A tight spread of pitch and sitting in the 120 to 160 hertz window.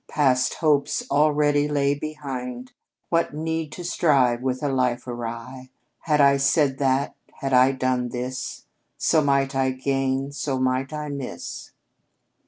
Yes: narrow, 2.3 semitones; low, 135 Hz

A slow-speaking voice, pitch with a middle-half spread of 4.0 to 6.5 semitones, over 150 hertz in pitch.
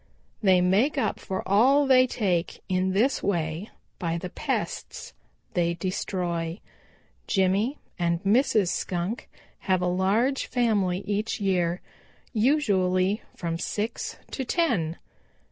Yes: slow, 115 wpm; average, 4.3 semitones; high, 190 Hz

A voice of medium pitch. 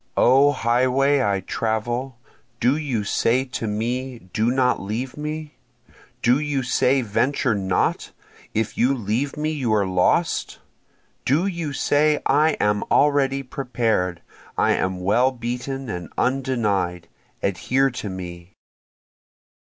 No: low, 125 Hz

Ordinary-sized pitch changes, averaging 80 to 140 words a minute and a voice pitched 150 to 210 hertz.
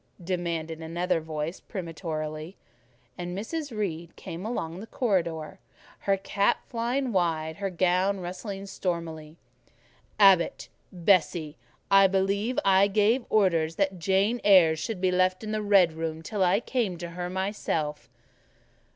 Yes: average, 3.3 semitones; slow, 135 wpm; medium, 185 Hz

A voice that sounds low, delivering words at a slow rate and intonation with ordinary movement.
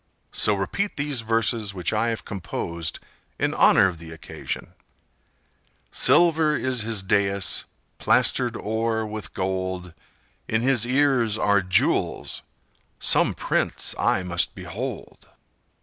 Yes: low, 105 Hz; slow, 115 wpm; average, 4.0 semitones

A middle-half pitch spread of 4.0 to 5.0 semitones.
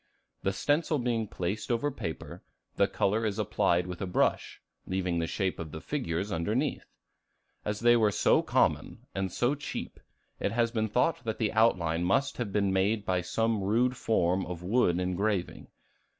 Yes: average, 4.4 semitones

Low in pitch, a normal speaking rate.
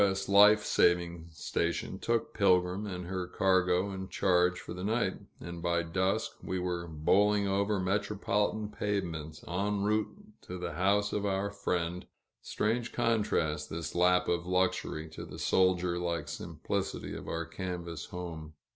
Yes: very low, 90 Hz; average, 145 wpm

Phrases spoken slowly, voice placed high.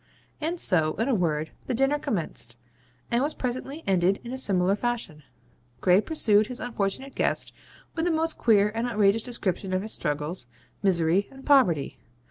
No: average, 165 wpm; high, 210 Hz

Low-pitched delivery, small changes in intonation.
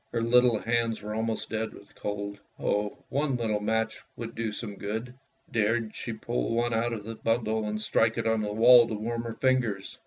Yes: low, 115 Hz; narrow, 1.6 semitones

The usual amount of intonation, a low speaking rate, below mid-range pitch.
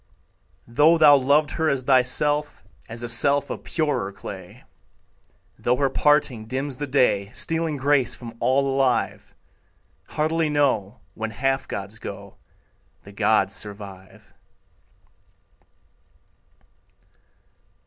Yes: average, 4.6 semitones; slow, 105 wpm; low, 130 Hz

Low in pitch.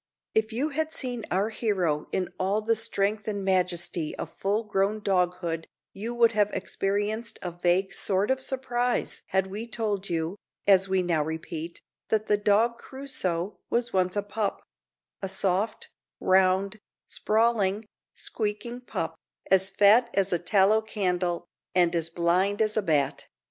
No: high, 200 Hz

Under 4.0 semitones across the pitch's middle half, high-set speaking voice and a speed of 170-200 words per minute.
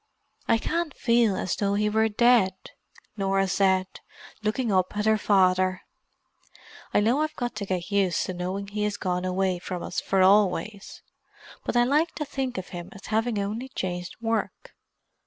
Yes: average, 3.4 semitones; high, 200 Hz; average, 175 wpm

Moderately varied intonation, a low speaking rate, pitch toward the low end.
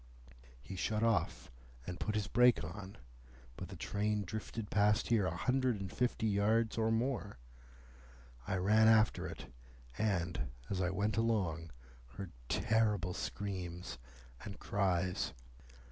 Yes: average, 3.2 semitones; slow, 130 wpm; low, 105 Hz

